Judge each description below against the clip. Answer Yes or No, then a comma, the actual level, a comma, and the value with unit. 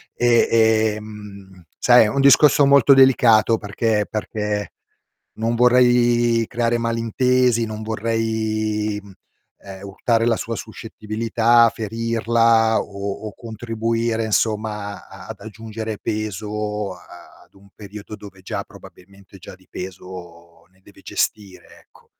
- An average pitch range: No, narrow, 2.0 semitones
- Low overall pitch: Yes, low, 110 Hz